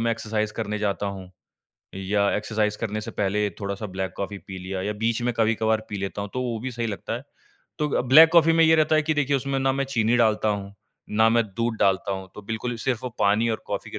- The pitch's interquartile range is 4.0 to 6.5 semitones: No, average, 3.2 semitones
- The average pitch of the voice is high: No, low, 110 Hz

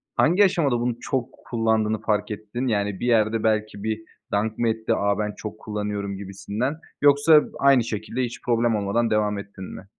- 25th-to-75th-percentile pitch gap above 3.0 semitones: No, narrow, 2.6 semitones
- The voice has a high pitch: No, low, 110 Hz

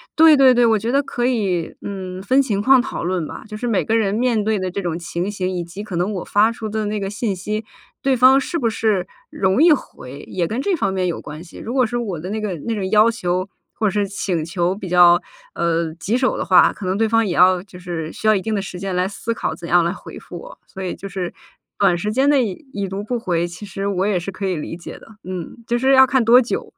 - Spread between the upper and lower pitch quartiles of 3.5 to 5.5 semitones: Yes, average, 4.0 semitones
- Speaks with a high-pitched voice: Yes, high, 200 Hz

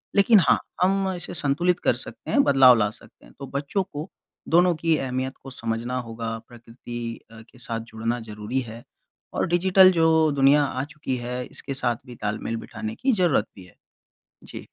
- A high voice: No, low, 135 Hz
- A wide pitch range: Yes, wide, 6.7 semitones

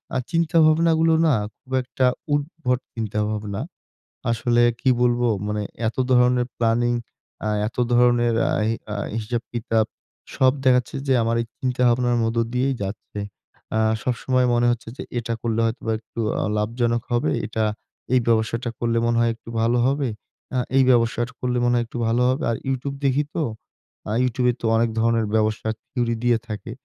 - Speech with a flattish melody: Yes, narrow, 1.9 semitones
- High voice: No, low, 120 Hz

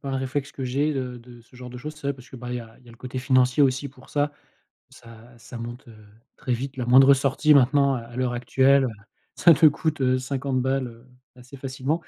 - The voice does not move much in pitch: Yes, narrow, 2.1 semitones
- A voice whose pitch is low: Yes, low, 130 Hz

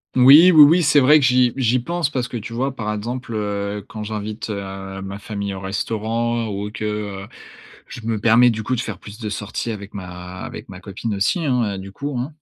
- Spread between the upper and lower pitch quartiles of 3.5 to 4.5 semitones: Yes, average, 3.8 semitones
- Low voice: Yes, low, 110 Hz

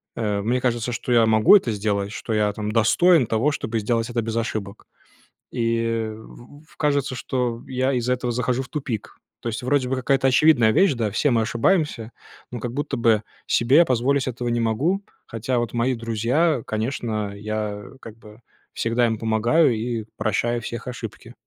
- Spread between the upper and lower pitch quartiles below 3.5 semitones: Yes, narrow, 2.6 semitones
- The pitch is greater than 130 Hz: No, low, 120 Hz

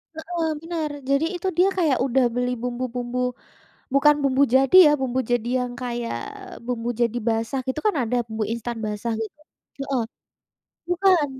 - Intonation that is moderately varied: Yes, average, 3.9 semitones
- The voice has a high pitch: Yes, very high, 255 Hz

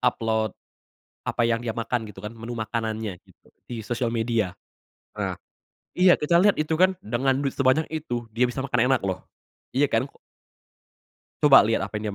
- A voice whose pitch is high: No, low, 120 Hz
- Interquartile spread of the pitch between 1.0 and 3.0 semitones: No, average, 3.4 semitones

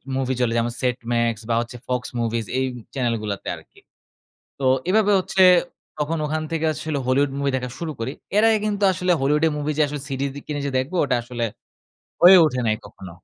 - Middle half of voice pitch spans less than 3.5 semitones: No, average, 4.7 semitones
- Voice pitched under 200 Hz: Yes, low, 135 Hz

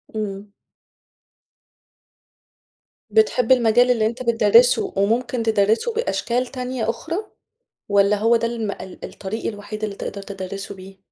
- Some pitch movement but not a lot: Yes, average, 3.1 semitones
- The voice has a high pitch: Yes, high, 220 Hz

